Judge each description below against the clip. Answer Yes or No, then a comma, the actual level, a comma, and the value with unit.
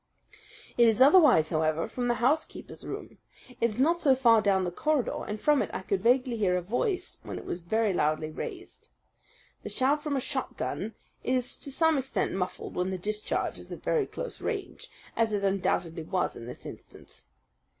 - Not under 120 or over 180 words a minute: No, average, 190 wpm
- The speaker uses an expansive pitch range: Yes, wide, 6.6 semitones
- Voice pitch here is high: Yes, high, 230 Hz